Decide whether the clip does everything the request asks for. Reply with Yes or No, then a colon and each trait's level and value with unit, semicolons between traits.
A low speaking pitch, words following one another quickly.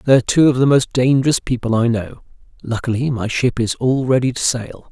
Yes: low, 125 Hz; fast, 210 wpm